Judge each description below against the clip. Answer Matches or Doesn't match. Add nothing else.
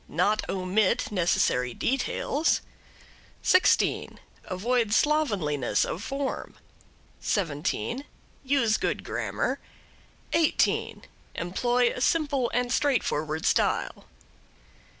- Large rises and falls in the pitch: Matches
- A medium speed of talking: Doesn't match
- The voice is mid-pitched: Doesn't match